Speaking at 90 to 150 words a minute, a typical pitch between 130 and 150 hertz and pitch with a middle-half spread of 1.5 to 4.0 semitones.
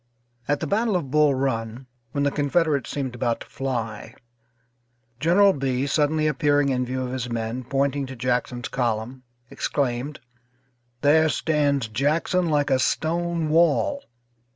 Yes: average, 140 wpm; medium, 140 Hz; average, 3.4 semitones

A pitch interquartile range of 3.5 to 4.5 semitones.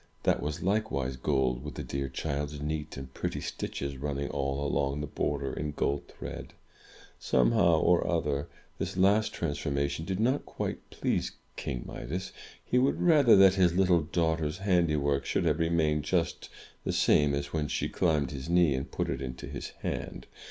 Yes: average, 3.9 semitones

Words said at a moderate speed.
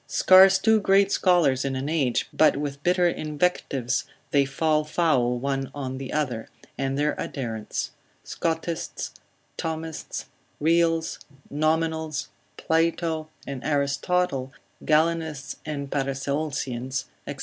No: slow, 110 wpm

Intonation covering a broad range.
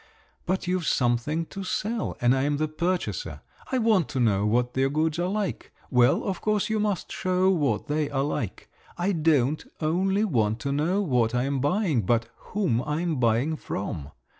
Yes: wide, 7.0 semitones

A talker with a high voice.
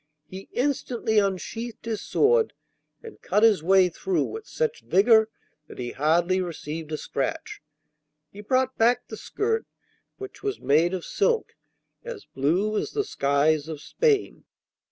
Yes: high, 210 Hz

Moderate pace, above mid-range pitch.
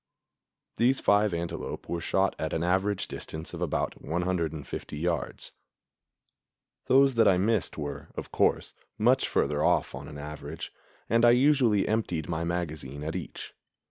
No: average, 145 wpm; very low, 85 Hz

